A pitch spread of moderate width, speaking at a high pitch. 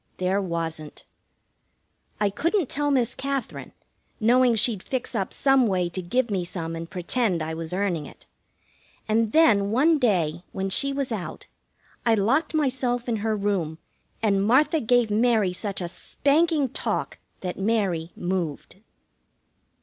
No: wide, 5.8 semitones; high, 215 Hz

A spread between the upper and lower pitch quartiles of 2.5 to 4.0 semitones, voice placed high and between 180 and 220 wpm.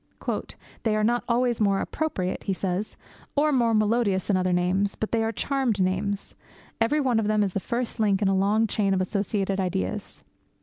Yes: average, 3.2 semitones; high, 210 Hz; average, 190 wpm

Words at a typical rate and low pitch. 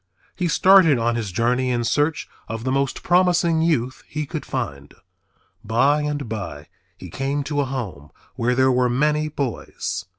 Yes: average, 165 wpm; low, 130 Hz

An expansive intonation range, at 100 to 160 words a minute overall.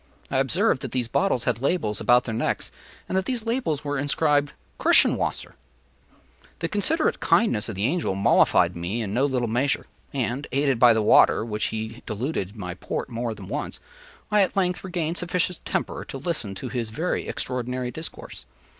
No: wide, 6.7 semitones; average, 180 wpm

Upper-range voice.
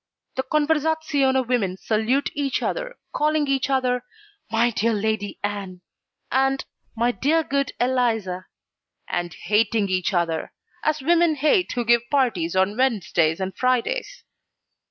Yes: high, 245 Hz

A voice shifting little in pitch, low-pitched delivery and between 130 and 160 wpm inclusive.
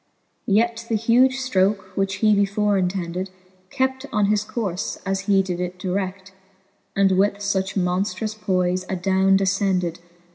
No: narrow, 2.1 semitones; high, 195 Hz; average, 140 wpm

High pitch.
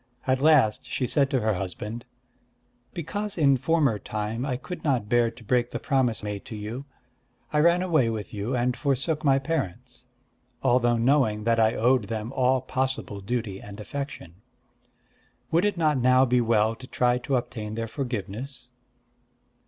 No: low, 125 Hz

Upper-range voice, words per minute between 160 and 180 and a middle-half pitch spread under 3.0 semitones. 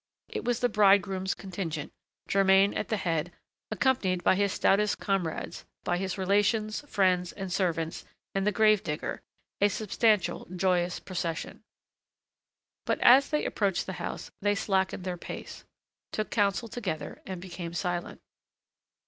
No: high, 195 Hz; average, 140 wpm; narrow, 2.6 semitones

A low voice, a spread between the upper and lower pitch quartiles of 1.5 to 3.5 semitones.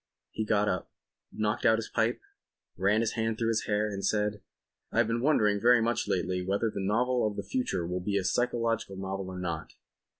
Yes: low, 105 Hz; average, 2.9 semitones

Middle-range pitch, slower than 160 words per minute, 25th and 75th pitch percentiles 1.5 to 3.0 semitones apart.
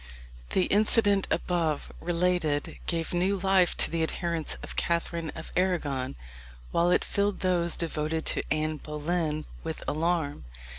Yes: medium, 170 Hz; slow, 135 wpm; narrow, 2.6 semitones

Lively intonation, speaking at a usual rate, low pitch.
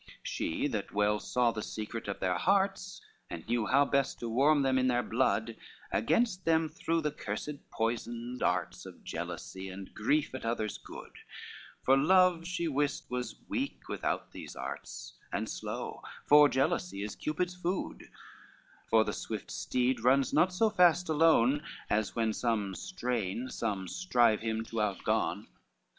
Yes: wide, 6.2 semitones; average, 155 wpm; low, 125 Hz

